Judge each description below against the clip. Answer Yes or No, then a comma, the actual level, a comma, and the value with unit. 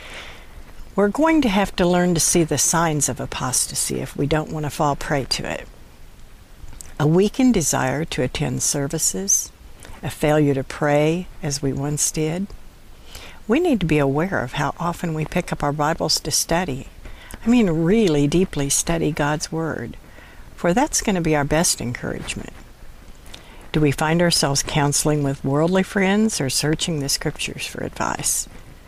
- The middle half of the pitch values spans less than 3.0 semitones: No, average, 3.6 semitones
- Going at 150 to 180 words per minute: Yes, average, 165 wpm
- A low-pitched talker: No, medium, 155 Hz